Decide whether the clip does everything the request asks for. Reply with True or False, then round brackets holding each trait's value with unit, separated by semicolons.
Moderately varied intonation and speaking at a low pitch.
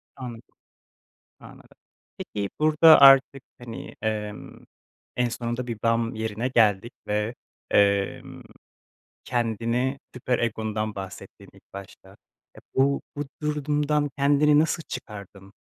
True (4.5 semitones; 120 Hz)